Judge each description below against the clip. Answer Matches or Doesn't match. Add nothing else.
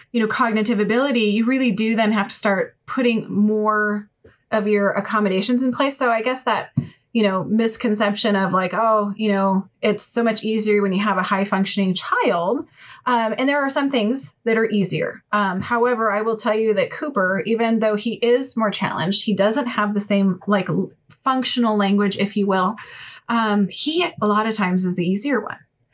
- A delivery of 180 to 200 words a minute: Matches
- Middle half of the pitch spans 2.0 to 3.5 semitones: Matches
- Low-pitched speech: Doesn't match